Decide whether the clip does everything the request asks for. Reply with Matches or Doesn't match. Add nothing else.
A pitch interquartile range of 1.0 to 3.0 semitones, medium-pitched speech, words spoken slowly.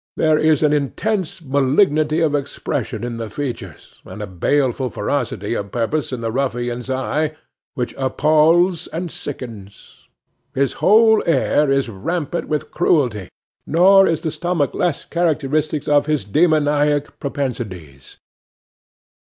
Doesn't match